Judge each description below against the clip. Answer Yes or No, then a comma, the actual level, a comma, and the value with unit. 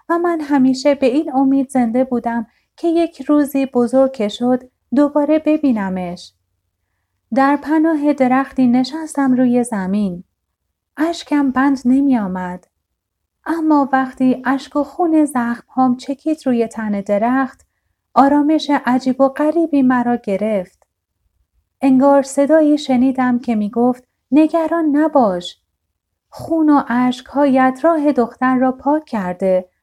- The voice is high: Yes, very high, 260 Hz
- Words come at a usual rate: Yes, average, 120 wpm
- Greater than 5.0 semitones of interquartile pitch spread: No, average, 3.8 semitones